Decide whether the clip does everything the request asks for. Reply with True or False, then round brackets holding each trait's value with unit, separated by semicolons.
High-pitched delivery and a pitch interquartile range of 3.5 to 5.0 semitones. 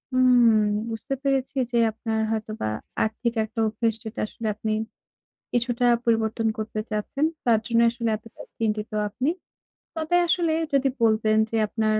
False (225 Hz; 2.4 semitones)